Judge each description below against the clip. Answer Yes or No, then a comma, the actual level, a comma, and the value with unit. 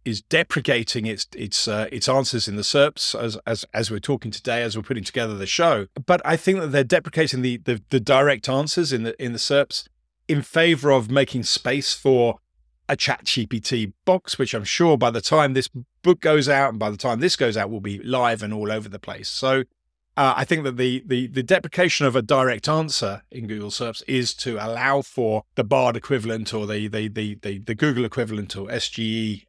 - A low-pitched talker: Yes, low, 125 Hz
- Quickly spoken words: Yes, fast, 215 wpm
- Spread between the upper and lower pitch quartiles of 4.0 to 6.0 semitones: Yes, average, 4.3 semitones